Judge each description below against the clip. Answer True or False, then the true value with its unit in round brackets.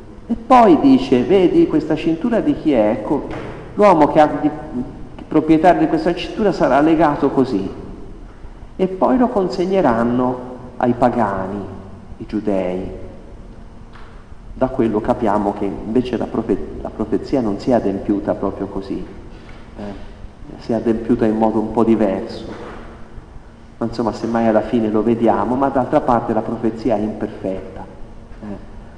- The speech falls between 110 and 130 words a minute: False (140 wpm)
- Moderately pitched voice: False (115 Hz)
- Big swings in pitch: True (6.2 semitones)